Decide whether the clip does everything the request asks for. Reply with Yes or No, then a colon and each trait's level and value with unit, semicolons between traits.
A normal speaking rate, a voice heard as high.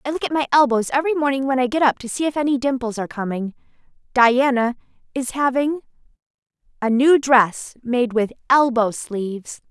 Yes: average, 175 wpm; very high, 255 Hz